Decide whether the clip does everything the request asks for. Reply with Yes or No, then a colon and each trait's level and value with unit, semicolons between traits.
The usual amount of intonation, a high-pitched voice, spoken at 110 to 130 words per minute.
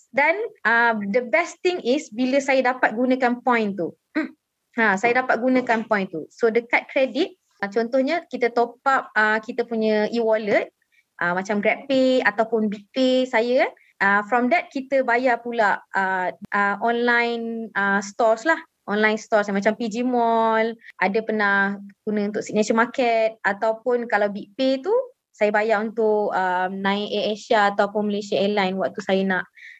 No: average, 3.7 semitones; high, 230 Hz; fast, 155 wpm